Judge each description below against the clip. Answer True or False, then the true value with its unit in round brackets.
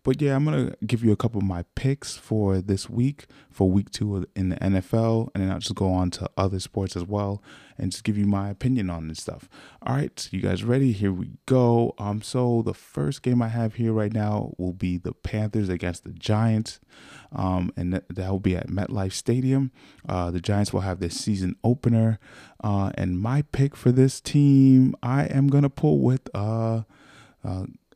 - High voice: False (105 Hz)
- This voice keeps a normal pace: False (215 wpm)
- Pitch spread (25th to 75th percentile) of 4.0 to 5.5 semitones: True (4.6 semitones)